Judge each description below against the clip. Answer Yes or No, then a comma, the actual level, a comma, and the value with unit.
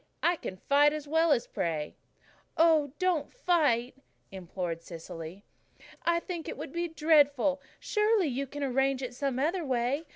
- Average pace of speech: Yes, average, 155 wpm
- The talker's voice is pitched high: Yes, very high, 280 Hz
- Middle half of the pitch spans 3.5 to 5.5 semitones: Yes, average, 5.1 semitones